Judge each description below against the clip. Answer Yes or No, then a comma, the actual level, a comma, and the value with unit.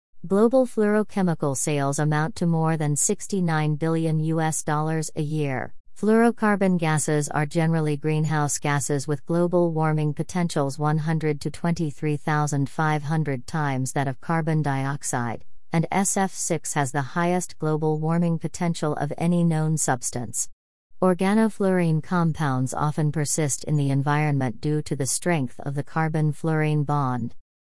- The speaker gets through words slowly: Yes, slow, 130 wpm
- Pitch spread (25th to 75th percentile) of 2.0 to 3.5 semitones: Yes, narrow, 2.5 semitones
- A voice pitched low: No, medium, 155 Hz